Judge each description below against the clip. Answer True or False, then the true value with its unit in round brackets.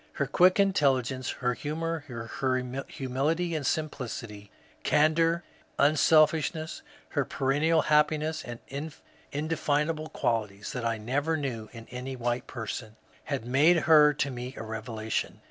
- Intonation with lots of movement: False (4.4 semitones)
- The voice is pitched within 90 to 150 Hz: True (140 Hz)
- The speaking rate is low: True (130 wpm)